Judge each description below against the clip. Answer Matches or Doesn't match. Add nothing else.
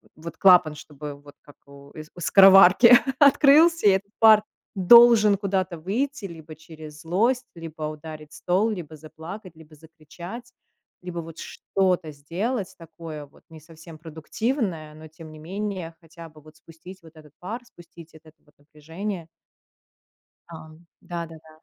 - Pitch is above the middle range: Doesn't match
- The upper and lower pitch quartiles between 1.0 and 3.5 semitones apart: Doesn't match